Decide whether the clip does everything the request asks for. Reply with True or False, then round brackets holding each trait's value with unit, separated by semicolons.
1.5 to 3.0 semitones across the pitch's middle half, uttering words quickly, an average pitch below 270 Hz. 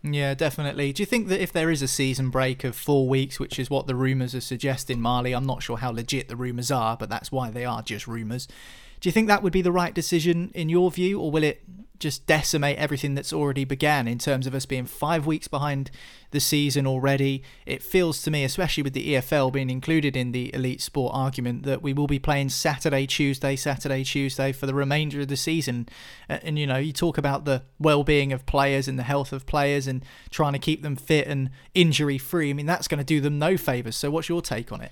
True (2.7 semitones; 240 wpm; 140 Hz)